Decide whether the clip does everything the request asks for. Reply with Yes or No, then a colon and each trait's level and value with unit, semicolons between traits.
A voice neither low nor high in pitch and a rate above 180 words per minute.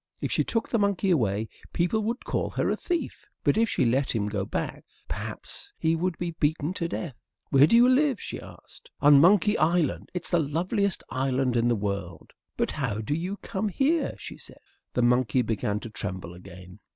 Yes: medium, 150 Hz; average, 200 wpm